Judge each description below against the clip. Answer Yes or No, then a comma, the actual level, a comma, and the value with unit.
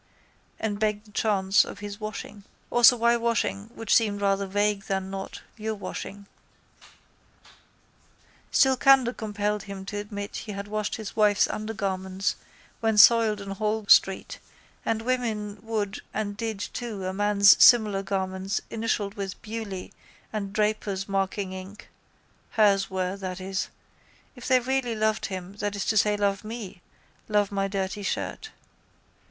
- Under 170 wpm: Yes, average, 145 wpm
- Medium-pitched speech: No, high, 205 Hz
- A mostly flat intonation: Yes, narrow, 1.9 semitones